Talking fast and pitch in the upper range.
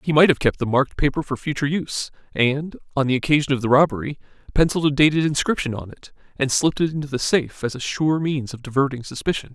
No: fast, 225 wpm; medium, 140 Hz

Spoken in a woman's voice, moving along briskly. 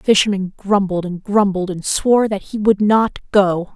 No: female; average, 190 wpm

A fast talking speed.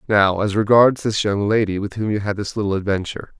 Yes: fast, 230 wpm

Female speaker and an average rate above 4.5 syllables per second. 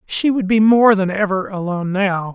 No: male; 5.0 syllables/s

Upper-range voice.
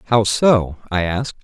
No: low, 105 Hz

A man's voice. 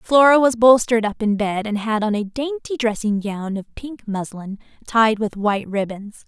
No: female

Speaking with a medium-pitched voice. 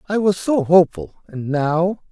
Yes: medium, 175 Hz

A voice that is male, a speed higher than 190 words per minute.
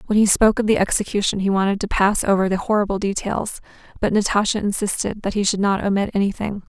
No: female; fast, 205 wpm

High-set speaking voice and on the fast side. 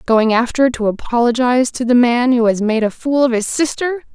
Yes: high, 245 Hz; fast, 215 wpm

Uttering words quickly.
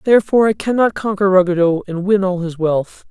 No: average, 195 wpm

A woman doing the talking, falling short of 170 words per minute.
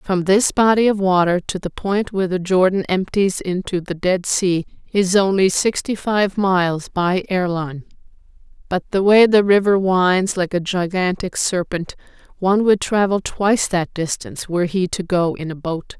No: female; average, 175 wpm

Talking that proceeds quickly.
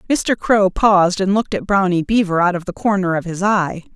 Yes: fast, 225 wpm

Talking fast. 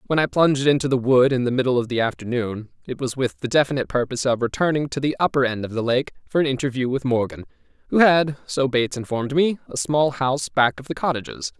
Yes: fast, 235 wpm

